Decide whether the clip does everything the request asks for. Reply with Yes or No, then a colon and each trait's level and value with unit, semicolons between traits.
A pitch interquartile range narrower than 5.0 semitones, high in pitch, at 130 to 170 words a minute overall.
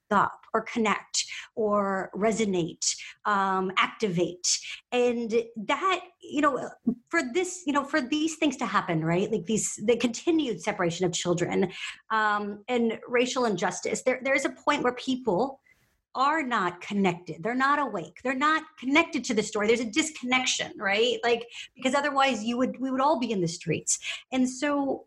No: wide, 5.4 semitones; high, 240 Hz; average, 165 wpm